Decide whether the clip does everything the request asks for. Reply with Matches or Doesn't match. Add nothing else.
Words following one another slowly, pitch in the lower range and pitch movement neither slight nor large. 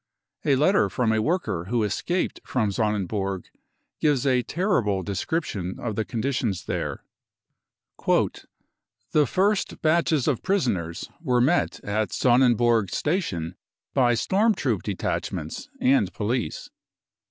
Doesn't match